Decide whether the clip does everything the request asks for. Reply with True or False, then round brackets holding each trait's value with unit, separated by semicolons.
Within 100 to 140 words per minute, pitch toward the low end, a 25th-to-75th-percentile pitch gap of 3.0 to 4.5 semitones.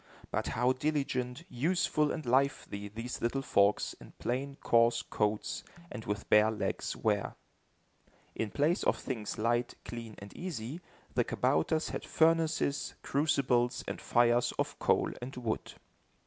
True (135 wpm; 125 Hz; 3.9 semitones)